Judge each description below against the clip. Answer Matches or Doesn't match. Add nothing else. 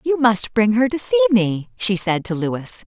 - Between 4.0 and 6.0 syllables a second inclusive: Matches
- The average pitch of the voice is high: Matches